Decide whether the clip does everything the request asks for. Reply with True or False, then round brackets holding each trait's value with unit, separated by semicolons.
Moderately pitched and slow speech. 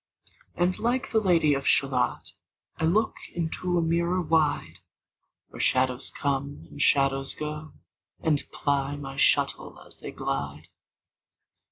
True (150 Hz; 130 wpm)